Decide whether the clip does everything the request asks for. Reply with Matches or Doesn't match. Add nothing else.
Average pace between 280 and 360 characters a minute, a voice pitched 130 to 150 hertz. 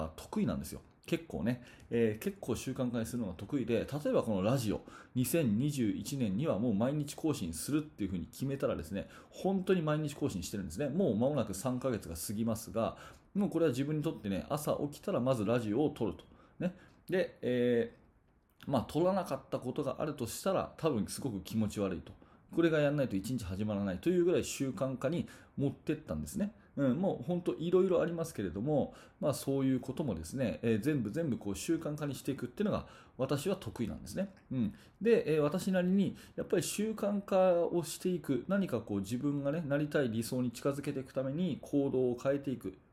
Doesn't match